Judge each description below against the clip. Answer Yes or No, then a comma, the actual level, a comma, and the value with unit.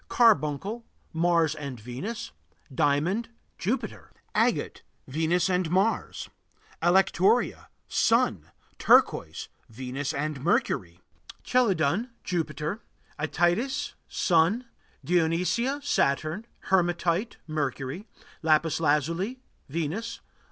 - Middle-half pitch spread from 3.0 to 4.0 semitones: No, wide, 5.4 semitones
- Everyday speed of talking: No, slow, 80 wpm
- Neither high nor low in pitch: Yes, medium, 170 Hz